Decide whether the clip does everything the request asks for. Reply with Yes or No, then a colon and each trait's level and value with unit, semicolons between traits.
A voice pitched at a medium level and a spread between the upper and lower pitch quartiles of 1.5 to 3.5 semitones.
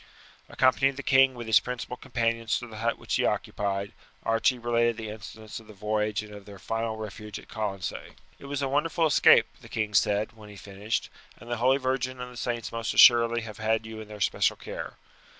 No: low, 115 Hz; narrow, 2.6 semitones